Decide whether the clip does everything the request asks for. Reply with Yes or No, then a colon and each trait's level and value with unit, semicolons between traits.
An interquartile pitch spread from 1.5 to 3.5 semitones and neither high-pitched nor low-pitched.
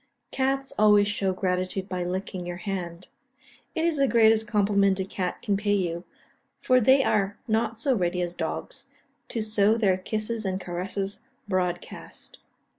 No: average, 3.0 semitones; high, 200 Hz